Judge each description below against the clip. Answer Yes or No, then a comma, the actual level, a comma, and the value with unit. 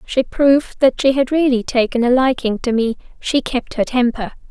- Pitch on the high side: Yes, very high, 250 Hz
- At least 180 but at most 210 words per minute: Yes, average, 200 wpm